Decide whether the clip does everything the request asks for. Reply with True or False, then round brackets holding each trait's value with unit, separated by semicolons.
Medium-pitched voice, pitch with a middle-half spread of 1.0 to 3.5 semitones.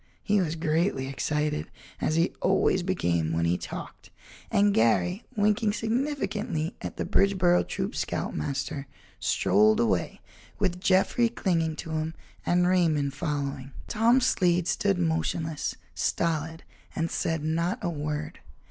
False (165 Hz; 4.2 semitones)